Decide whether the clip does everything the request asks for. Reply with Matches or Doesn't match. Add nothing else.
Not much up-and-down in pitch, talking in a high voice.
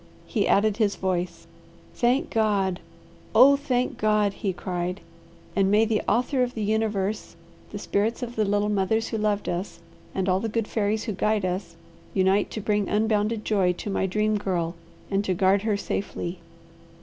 Matches